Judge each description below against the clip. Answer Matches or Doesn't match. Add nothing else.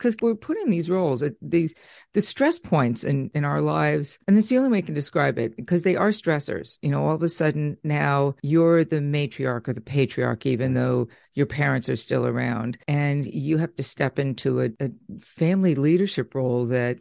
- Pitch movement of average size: Matches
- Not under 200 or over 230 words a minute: Matches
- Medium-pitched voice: Matches